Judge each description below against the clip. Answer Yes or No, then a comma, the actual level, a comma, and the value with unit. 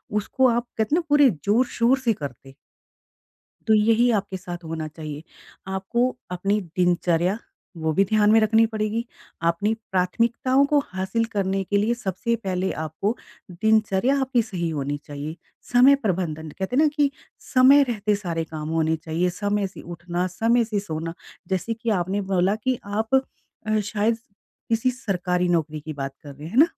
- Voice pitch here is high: Yes, high, 200 Hz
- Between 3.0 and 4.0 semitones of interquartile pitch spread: No, average, 4.8 semitones